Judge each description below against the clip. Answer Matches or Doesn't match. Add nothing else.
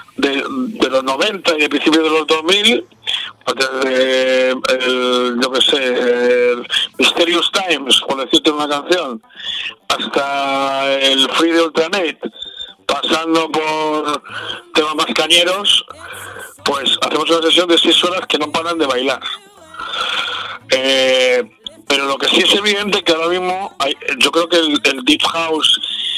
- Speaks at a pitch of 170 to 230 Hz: Doesn't match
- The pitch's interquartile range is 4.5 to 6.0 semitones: Matches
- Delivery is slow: Doesn't match